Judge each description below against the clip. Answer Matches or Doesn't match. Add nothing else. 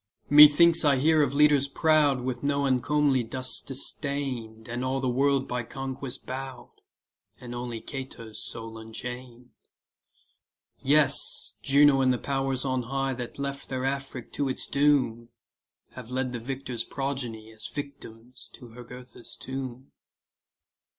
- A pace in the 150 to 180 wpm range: Doesn't match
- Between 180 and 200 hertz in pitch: Doesn't match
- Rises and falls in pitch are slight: Matches